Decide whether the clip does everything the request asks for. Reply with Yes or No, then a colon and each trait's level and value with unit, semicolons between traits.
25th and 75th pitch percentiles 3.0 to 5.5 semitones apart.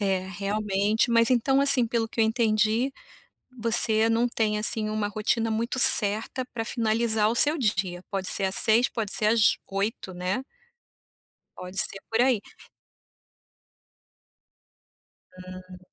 No: narrow, 2.6 semitones